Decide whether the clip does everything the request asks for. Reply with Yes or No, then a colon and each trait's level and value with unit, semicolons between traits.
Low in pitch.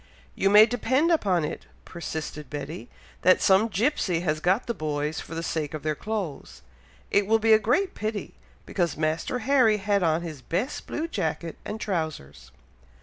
No: medium, 185 Hz